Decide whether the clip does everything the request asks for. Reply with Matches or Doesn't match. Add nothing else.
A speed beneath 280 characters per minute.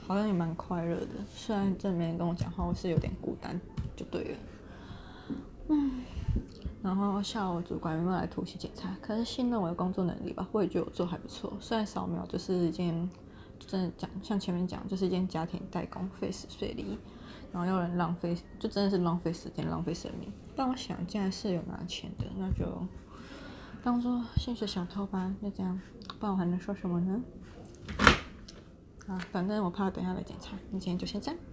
Doesn't match